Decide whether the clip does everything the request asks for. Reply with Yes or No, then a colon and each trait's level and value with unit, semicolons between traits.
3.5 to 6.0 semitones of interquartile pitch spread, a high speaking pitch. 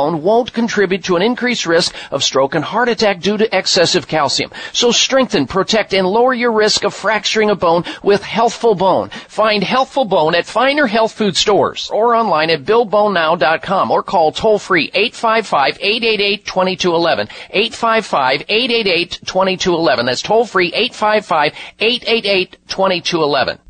Yes: average, 4.0 semitones; high, 205 Hz